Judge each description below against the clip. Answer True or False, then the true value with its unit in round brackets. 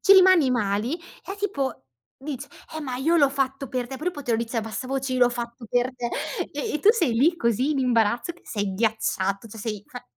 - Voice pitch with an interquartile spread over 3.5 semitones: True (4.0 semitones)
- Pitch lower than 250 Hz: False (255 Hz)